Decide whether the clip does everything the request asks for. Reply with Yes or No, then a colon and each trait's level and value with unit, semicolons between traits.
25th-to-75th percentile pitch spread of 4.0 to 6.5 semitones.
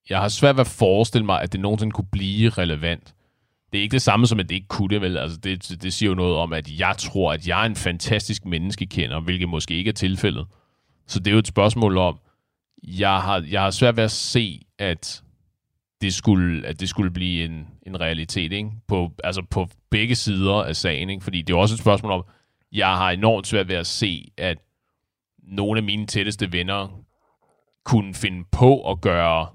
No: average, 3.0 semitones